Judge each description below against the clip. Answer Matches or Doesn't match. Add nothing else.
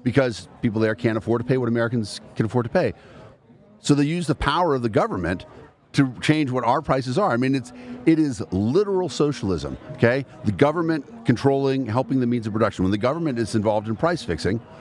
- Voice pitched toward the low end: Matches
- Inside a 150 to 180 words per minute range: Doesn't match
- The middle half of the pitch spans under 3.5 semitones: Doesn't match